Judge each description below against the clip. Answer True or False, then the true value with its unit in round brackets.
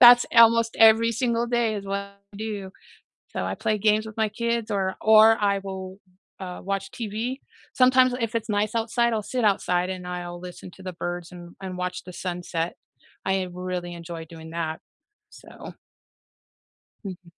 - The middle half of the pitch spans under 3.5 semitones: False (3.8 semitones)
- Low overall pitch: False (200 Hz)